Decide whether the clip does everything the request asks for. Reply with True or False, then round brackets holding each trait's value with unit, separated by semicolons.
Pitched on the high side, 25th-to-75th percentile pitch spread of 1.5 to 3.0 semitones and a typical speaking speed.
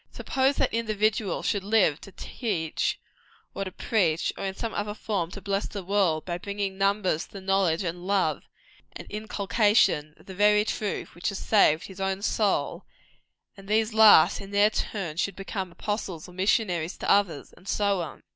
True (195 Hz; 2.7 semitones; 180 wpm)